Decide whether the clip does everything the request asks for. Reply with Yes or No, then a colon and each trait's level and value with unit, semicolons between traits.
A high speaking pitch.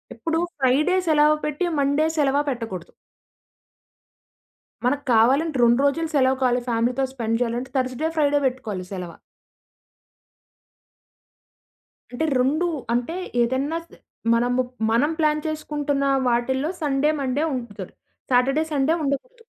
Yes: very high, 270 Hz